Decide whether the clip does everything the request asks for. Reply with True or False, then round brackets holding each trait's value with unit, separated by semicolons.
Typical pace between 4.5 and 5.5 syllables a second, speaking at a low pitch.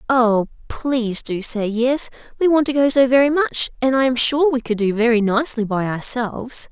False (4.9 syllables/s; 245 Hz)